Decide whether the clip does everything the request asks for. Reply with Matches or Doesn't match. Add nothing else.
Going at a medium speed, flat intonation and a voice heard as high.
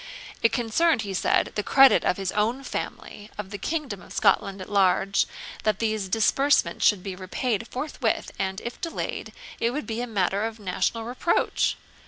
Doesn't match